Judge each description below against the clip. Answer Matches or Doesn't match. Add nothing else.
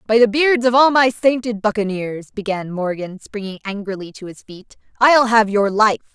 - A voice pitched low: Doesn't match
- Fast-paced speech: Doesn't match